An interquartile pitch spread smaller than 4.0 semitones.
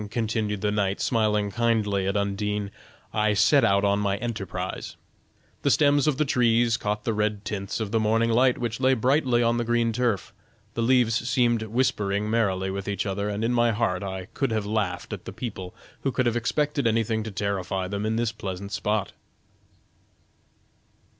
Yes: average, 2.7 semitones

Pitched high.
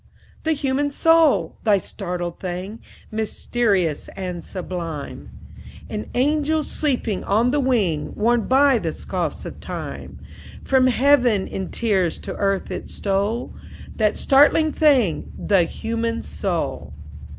Yes: high, 225 Hz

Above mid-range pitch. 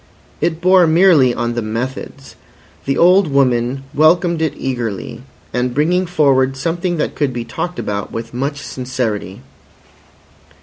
No: low, 135 Hz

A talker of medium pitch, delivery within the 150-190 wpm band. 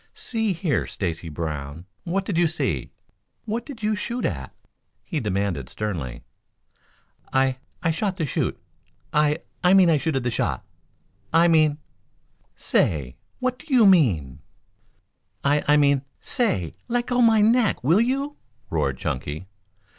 No: medium, 155 Hz; average, 140 wpm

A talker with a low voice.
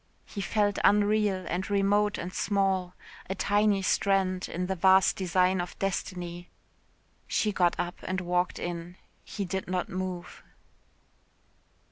No: high, 190 Hz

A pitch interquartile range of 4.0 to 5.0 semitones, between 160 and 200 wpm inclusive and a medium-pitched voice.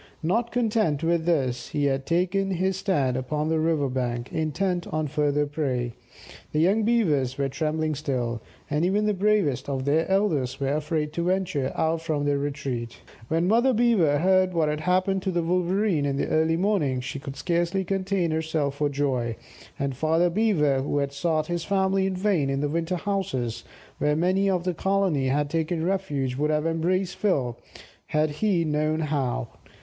Yes: average, 4.7 semitones; average, 180 wpm; medium, 160 Hz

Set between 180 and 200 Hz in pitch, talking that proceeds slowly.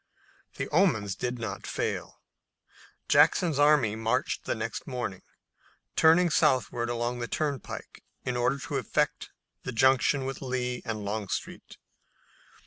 No: low, 125 Hz; slow, 125 wpm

